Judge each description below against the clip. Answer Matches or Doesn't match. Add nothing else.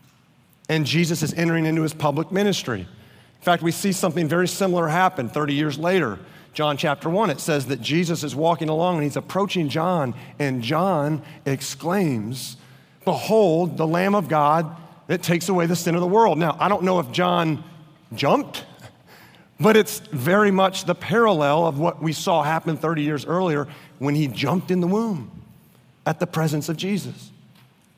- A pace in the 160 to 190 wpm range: Matches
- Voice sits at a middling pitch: Matches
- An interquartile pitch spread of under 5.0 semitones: Matches